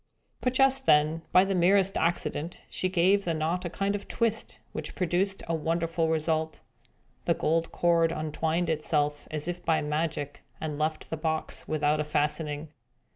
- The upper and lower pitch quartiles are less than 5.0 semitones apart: Yes, narrow, 2.5 semitones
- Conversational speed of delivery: Yes, average, 165 wpm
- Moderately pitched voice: Yes, medium, 165 Hz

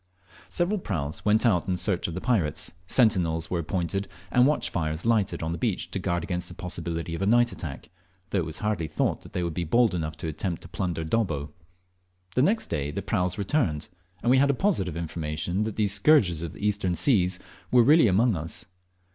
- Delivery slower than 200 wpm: No, fast, 205 wpm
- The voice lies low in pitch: Yes, very low, 90 Hz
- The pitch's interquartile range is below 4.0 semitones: No, average, 5.2 semitones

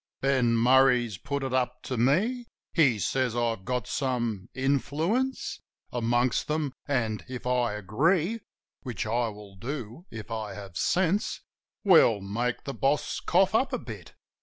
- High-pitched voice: No, low, 125 Hz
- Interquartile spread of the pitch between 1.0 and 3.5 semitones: No, average, 3.9 semitones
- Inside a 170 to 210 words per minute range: No, average, 155 wpm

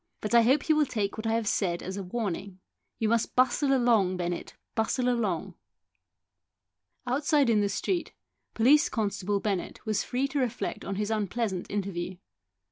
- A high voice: Yes, high, 220 Hz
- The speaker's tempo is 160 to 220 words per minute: Yes, average, 165 wpm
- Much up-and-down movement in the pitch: No, average, 4.0 semitones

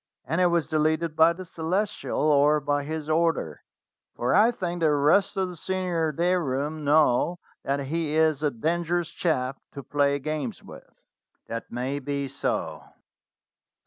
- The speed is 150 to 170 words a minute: Yes, average, 155 wpm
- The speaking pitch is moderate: Yes, medium, 155 Hz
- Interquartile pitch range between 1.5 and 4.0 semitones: Yes, average, 3.1 semitones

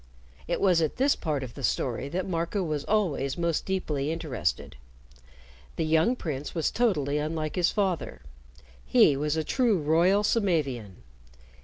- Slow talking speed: No, average, 150 wpm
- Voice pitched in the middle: Yes, medium, 160 Hz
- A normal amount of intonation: Yes, average, 4.4 semitones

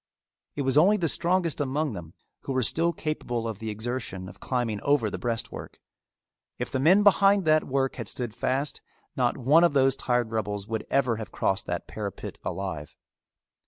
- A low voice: Yes, low, 130 Hz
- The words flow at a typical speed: Yes, average, 180 wpm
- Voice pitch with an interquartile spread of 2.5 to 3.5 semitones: No, wide, 5.5 semitones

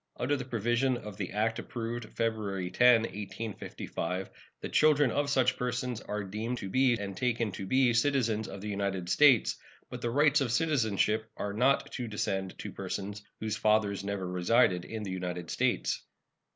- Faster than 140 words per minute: Yes, average, 170 wpm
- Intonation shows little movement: No, average, 3.9 semitones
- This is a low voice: Yes, low, 110 Hz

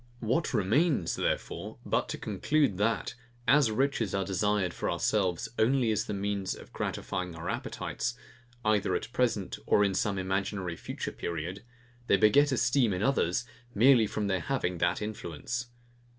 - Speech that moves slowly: No, average, 150 wpm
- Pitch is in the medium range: No, low, 105 Hz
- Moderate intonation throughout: Yes, average, 4.4 semitones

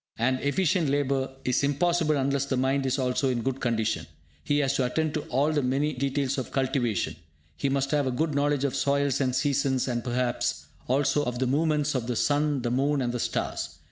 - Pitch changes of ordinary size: No, narrow, 2.3 semitones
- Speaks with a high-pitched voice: No, low, 135 Hz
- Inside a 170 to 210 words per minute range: Yes, fast, 205 wpm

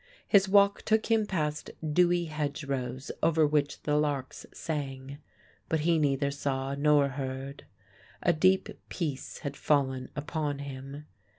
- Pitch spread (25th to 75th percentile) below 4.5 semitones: Yes, average, 2.7 semitones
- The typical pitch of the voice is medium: Yes, medium, 145 Hz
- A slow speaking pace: Yes, slow, 130 wpm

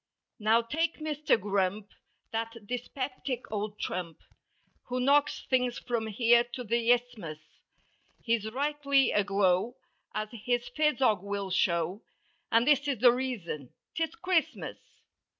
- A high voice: Yes, high, 235 Hz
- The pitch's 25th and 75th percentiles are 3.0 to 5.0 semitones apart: Yes, average, 4.3 semitones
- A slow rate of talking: Yes, slow, 120 wpm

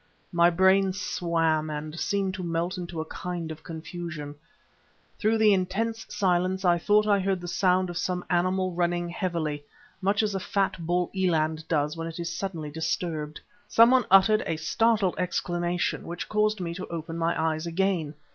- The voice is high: No, medium, 175 Hz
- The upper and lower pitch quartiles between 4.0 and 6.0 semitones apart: No, average, 2.7 semitones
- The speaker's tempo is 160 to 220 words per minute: Yes, average, 170 wpm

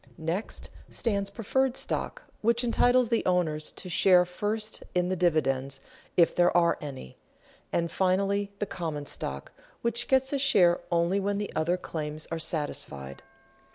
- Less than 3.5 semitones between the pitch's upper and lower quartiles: No, average, 4.8 semitones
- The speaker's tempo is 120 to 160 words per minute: Yes, average, 150 wpm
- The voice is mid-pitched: Yes, medium, 180 Hz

